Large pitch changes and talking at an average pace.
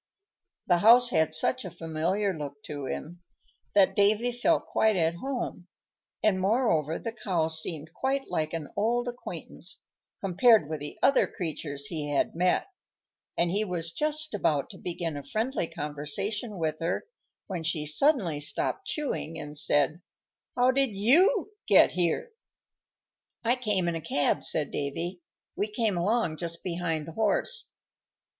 Yes: wide, 6.3 semitones; average, 150 wpm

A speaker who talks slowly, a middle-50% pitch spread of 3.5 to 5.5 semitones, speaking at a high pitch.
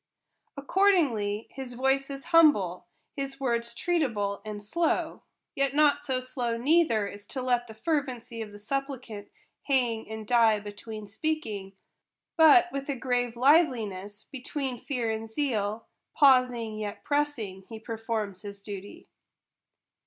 Yes: slow, 130 wpm; average, 4.5 semitones; high, 240 Hz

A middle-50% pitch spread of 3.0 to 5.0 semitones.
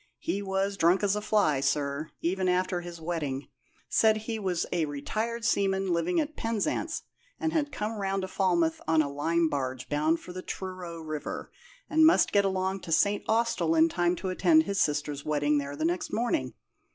Yes: average, 4.4 semitones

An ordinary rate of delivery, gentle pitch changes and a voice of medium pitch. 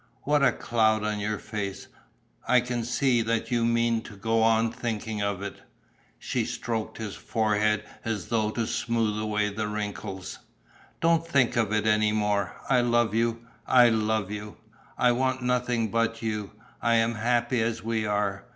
No: average, 170 wpm; narrow, 1.9 semitones; low, 110 Hz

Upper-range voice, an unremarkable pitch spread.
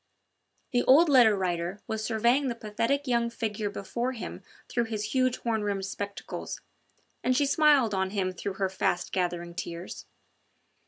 Yes: high, 220 Hz; average, 4.2 semitones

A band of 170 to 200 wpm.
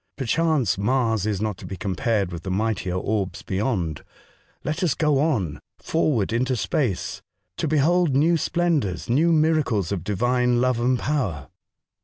No: average, 155 wpm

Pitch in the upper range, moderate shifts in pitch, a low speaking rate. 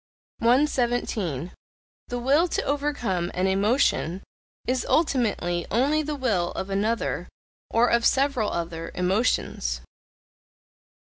No: high, 230 Hz; wide, 6.5 semitones; slow, 100 wpm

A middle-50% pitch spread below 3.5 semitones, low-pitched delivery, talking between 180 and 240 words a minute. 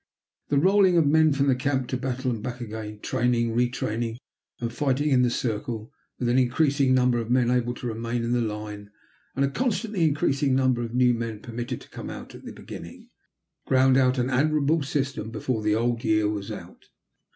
Yes: average, 2.9 semitones; low, 125 Hz; average, 195 wpm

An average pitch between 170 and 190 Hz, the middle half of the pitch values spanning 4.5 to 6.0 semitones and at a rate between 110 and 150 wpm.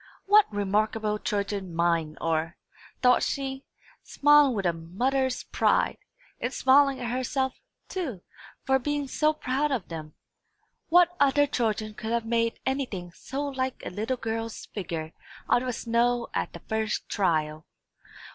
No: high, 235 Hz; average, 5.2 semitones; average, 140 wpm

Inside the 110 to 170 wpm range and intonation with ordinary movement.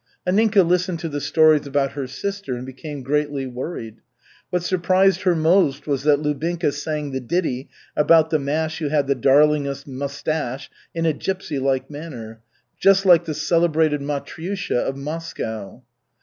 Yes: average, 160 wpm; average, 3.4 semitones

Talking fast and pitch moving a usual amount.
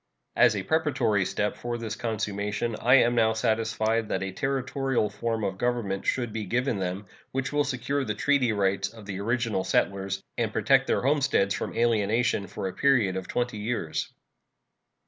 No: average, 170 wpm; average, 3.6 semitones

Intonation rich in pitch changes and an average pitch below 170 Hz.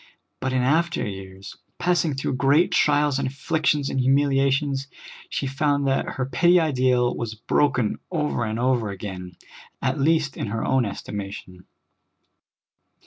No: average, 4.0 semitones; low, 135 Hz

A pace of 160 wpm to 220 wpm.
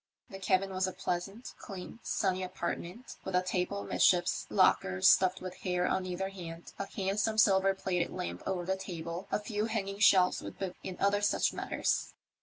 Yes: average, 180 wpm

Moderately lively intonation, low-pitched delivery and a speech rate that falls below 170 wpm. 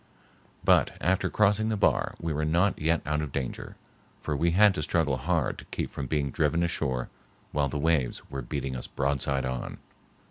No: average, 3.7 semitones; very low, 75 Hz; average, 185 wpm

